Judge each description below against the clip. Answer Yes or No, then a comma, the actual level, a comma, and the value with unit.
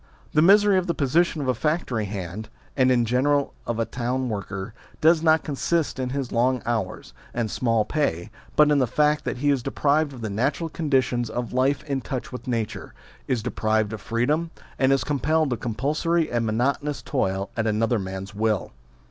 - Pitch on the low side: Yes, low, 130 Hz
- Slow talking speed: No, average, 190 wpm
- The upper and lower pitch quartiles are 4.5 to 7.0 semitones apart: Yes, average, 4.9 semitones